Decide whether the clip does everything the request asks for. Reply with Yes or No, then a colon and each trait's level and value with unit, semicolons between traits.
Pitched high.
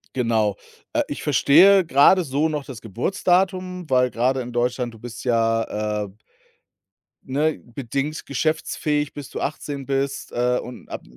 No: low, 135 Hz